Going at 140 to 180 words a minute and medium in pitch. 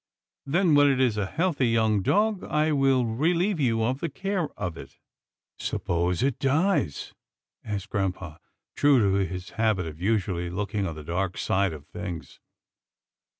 No: average, 155 wpm; low, 110 Hz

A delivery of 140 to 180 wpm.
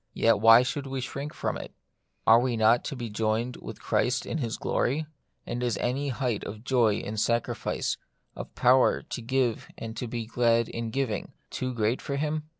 No: average, 190 wpm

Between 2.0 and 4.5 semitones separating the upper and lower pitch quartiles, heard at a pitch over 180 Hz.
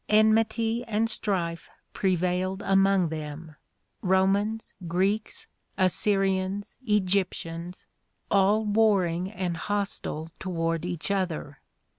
Yes: average, 3.0 semitones; high, 190 Hz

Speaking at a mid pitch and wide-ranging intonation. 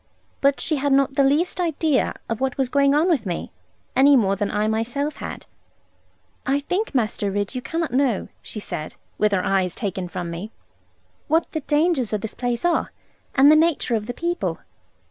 No: very high, 265 Hz; wide, 6.0 semitones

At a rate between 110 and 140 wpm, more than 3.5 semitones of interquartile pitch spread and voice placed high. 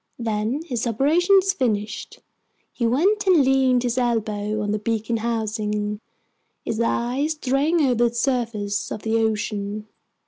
Yes: slow, 135 wpm; average, 3.9 semitones; high, 235 Hz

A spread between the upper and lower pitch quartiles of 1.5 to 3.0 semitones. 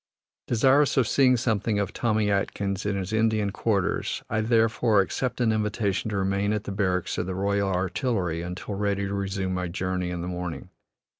Yes: narrow, 2.6 semitones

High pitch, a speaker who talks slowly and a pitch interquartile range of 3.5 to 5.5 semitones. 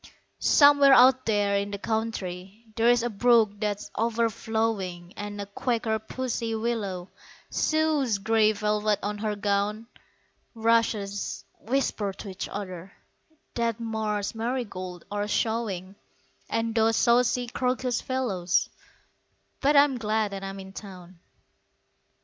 No: high, 220 Hz; slow, 120 wpm; narrow, 2.6 semitones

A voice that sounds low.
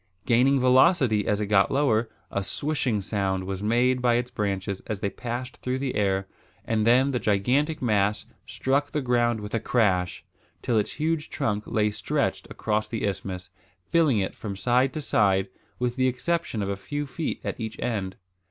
Yes: low, 115 Hz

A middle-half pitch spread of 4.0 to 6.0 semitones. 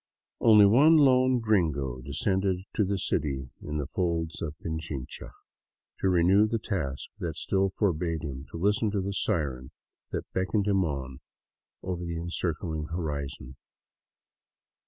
Yes: average, 5.1 semitones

